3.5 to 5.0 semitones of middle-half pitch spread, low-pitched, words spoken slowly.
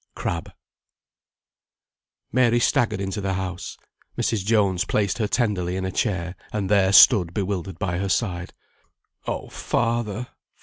No: average, 2.8 semitones; low, 100 Hz; slow, 130 wpm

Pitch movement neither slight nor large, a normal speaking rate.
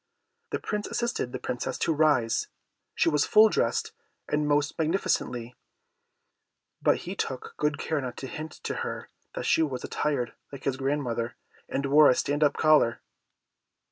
Yes: average, 3.4 semitones; average, 160 wpm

